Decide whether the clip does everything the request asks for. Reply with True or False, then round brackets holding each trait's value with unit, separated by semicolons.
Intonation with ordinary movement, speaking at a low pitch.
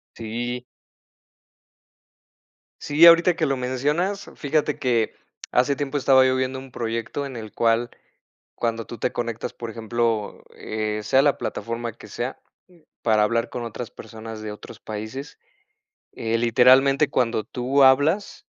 True (3.2 semitones; 120 Hz)